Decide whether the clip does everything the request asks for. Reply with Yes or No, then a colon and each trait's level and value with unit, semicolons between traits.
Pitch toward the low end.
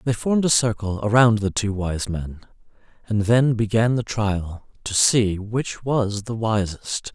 Yes: low, 110 Hz